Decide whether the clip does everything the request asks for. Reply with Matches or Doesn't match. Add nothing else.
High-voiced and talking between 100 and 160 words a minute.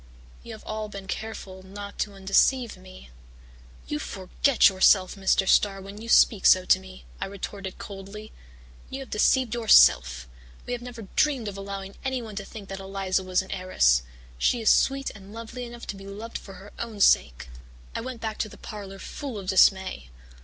Doesn't match